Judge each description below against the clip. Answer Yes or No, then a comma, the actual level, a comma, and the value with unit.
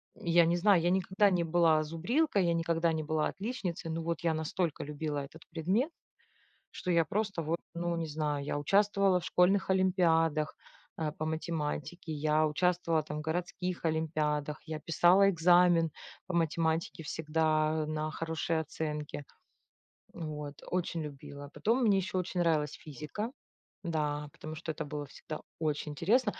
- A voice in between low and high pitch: Yes, medium, 165 Hz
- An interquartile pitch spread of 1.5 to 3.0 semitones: Yes, narrow, 2.6 semitones